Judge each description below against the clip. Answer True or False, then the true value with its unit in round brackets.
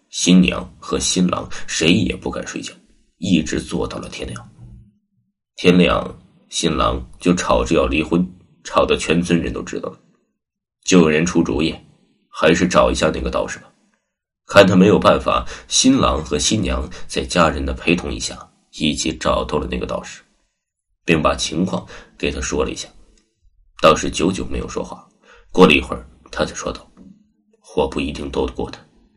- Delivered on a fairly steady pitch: True (2.3 semitones)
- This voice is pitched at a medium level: False (90 Hz)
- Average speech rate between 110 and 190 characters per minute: False (240 characters per minute)